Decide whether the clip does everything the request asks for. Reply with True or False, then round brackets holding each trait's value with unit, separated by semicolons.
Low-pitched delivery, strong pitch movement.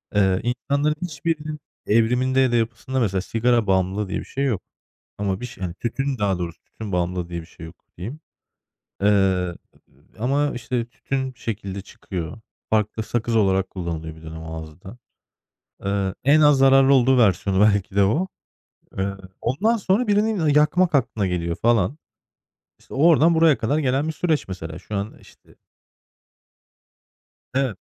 True (115 Hz; 6.3 semitones)